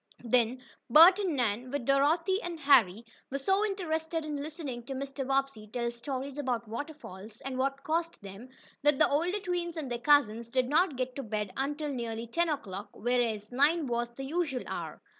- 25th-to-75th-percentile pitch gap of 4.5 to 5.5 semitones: Yes, average, 4.8 semitones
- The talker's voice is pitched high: Yes, very high, 275 Hz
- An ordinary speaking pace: Yes, average, 180 wpm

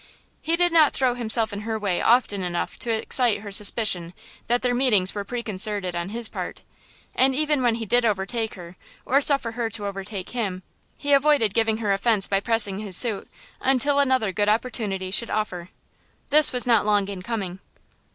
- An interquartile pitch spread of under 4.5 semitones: Yes, average, 3.8 semitones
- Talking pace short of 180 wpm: No, average, 185 wpm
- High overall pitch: Yes, high, 220 Hz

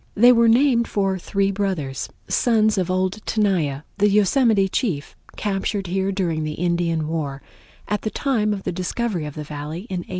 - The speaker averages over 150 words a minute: Yes, average, 175 wpm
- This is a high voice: Yes, high, 195 Hz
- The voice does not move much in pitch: No, average, 4.2 semitones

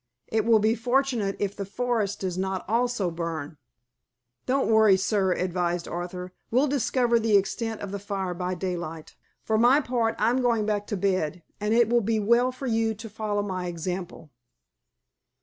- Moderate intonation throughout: Yes, average, 3.9 semitones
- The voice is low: No, high, 205 Hz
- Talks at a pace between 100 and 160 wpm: No, average, 170 wpm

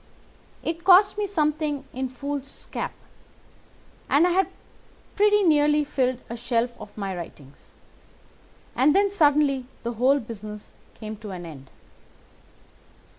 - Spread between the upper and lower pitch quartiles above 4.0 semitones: Yes, wide, 5.5 semitones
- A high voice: Yes, very high, 275 Hz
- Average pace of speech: No, slow, 125 wpm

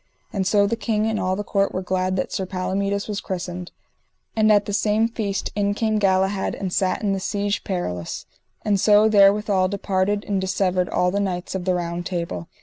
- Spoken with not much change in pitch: Yes, narrow, 1.9 semitones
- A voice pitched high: Yes, high, 195 Hz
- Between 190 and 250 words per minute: Yes, average, 200 wpm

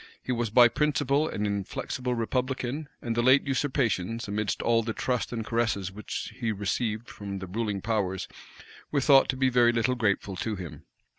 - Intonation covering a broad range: No, average, 3.7 semitones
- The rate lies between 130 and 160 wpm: No, average, 175 wpm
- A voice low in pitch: Yes, low, 115 Hz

